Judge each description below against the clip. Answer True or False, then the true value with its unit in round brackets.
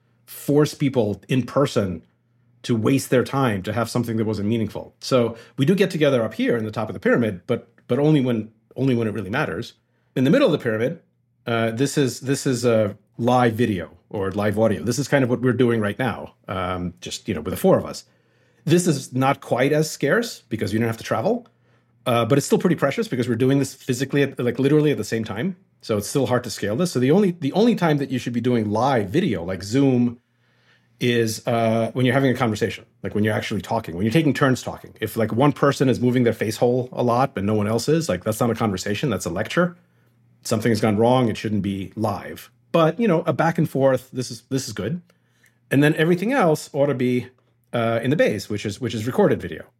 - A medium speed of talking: False (240 wpm)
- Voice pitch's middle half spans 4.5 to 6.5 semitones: False (3.7 semitones)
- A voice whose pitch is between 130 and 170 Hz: False (120 Hz)